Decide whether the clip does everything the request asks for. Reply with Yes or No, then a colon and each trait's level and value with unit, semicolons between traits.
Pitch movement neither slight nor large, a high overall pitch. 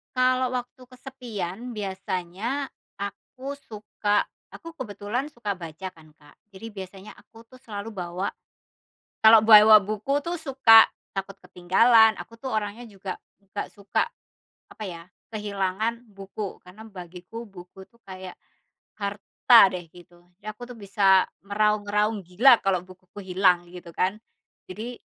Yes: average, 3.5 semitones; high, 205 Hz